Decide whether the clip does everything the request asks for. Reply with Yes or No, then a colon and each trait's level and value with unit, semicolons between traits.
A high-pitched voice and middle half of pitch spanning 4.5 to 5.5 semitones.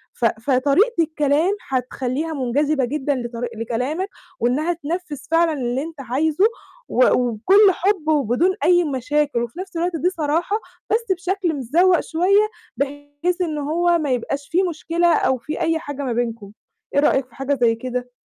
Yes: very high, 295 Hz; average, 5.2 semitones